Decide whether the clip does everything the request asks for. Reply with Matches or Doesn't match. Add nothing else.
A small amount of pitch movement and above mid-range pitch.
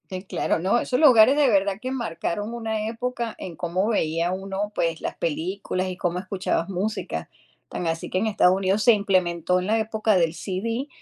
Doesn't match